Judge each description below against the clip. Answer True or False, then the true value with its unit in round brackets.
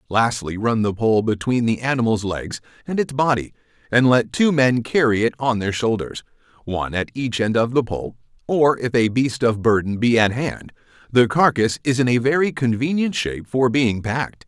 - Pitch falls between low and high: False (120 Hz)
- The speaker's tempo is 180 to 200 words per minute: True (195 wpm)